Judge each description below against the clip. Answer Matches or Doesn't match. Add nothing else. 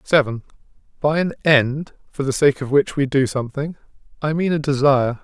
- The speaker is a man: Matches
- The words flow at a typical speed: Matches